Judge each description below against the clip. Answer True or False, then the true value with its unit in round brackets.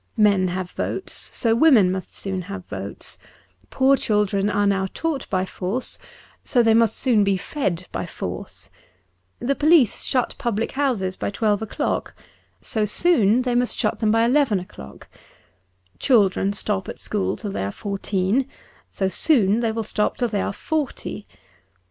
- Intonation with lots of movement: False (4.2 semitones)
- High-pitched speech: True (210 Hz)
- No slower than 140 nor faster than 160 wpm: True (155 wpm)